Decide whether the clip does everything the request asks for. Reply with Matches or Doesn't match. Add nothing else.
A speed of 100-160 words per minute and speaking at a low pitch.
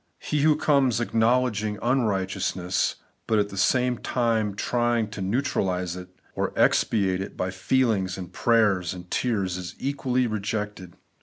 Matches